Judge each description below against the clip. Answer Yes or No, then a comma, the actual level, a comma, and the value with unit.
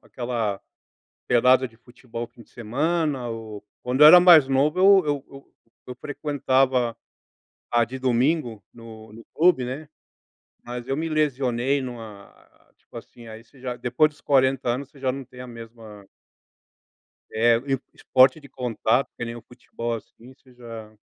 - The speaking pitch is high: No, low, 125 Hz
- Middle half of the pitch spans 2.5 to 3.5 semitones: Yes, average, 2.8 semitones